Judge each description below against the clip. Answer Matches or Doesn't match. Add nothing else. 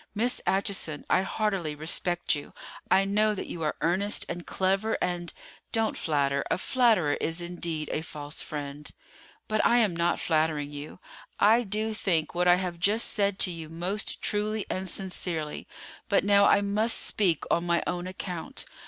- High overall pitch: Doesn't match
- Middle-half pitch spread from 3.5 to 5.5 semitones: Matches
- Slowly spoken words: Doesn't match